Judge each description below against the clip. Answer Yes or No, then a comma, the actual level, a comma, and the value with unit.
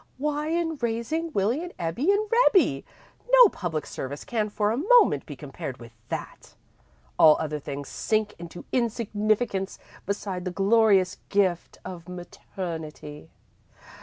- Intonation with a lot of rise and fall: Yes, wide, 6.7 semitones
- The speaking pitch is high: Yes, high, 200 Hz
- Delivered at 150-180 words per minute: No, slow, 135 wpm